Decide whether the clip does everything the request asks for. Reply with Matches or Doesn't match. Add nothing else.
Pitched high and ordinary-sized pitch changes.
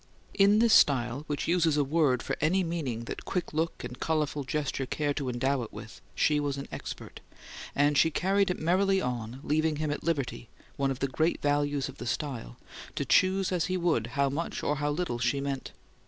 Doesn't match